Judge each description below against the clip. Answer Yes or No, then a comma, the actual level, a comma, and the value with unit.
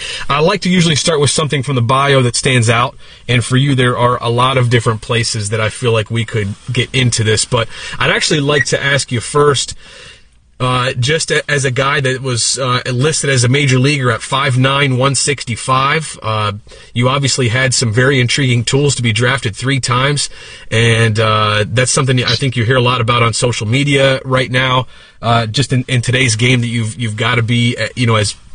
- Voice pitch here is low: Yes, low, 125 Hz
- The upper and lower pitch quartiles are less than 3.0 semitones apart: Yes, narrow, 2.6 semitones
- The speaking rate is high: Yes, fast, 220 wpm